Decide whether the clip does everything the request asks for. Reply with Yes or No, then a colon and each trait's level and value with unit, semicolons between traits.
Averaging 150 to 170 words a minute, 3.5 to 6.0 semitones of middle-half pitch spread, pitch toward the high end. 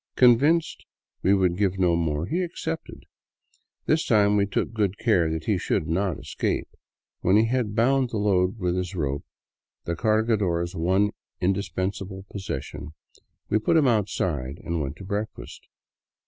No: average, 155 wpm; average, 4.1 semitones; low, 100 Hz